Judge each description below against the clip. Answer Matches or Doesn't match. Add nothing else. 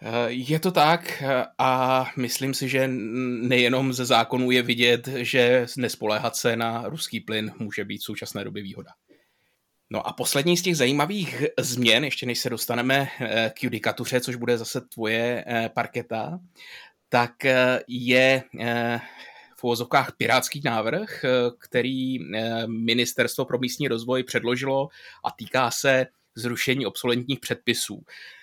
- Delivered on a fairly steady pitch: Matches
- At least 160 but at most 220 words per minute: Doesn't match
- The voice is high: Doesn't match